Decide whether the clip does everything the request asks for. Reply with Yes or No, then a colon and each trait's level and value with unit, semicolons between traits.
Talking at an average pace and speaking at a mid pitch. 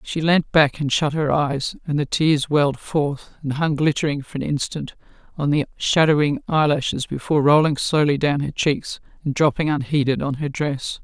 Yes: average, 190 wpm; medium, 145 Hz